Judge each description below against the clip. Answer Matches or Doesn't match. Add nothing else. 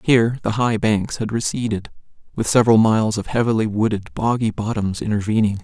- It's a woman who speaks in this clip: Doesn't match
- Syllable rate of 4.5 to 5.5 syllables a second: Doesn't match